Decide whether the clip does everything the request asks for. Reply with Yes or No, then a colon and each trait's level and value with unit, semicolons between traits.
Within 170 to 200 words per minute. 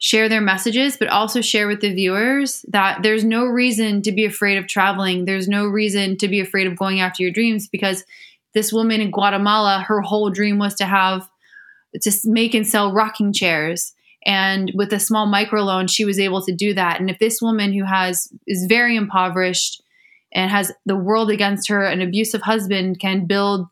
Yes: average, 195 wpm